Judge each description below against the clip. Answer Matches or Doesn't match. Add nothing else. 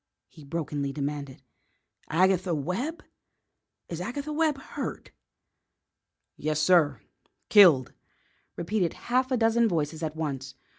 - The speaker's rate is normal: Doesn't match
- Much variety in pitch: Matches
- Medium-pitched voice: Matches